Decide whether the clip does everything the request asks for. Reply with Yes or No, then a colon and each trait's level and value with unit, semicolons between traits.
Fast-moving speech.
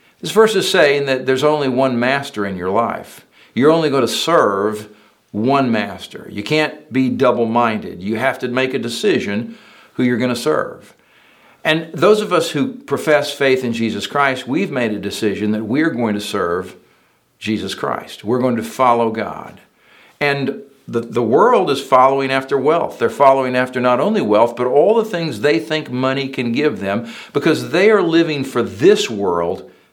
No: average, 185 wpm